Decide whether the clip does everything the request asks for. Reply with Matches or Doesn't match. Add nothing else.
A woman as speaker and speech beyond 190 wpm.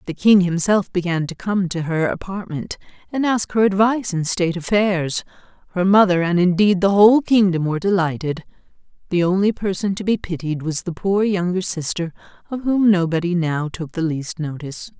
Doesn't match